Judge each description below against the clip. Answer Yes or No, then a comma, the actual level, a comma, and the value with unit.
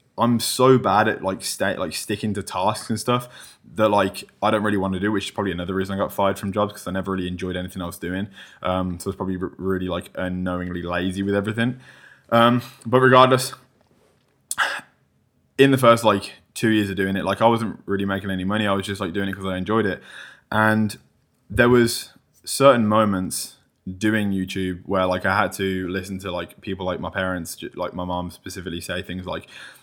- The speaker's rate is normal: No, fast, 210 wpm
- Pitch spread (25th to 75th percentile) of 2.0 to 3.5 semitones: Yes, average, 2.8 semitones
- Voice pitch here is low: Yes, low, 100 Hz